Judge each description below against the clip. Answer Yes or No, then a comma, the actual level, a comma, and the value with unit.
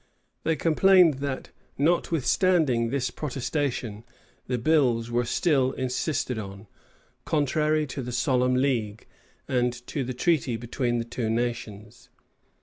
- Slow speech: Yes, slow, 120 wpm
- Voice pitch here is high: No, low, 125 Hz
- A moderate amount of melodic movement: Yes, average, 3.9 semitones